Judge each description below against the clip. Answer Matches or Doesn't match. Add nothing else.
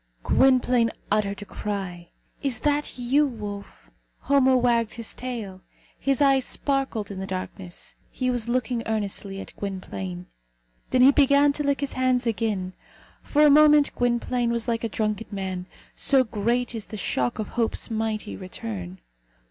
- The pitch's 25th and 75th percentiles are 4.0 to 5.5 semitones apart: Matches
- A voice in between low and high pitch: Doesn't match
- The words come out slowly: Doesn't match